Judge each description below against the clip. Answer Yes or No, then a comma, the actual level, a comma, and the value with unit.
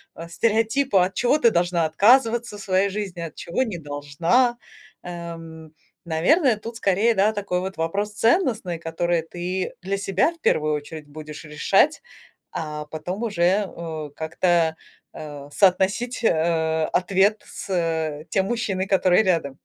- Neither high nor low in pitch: Yes, medium, 180 Hz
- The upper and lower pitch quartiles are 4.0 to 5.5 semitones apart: Yes, average, 4.5 semitones